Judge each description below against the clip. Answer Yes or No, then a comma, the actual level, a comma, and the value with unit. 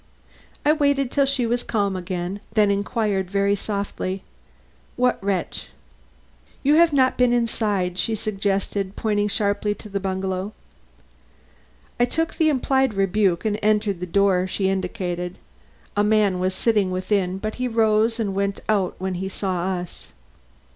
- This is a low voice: No, high, 200 Hz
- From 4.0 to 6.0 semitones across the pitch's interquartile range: No, average, 3.0 semitones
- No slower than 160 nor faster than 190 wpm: No, average, 150 wpm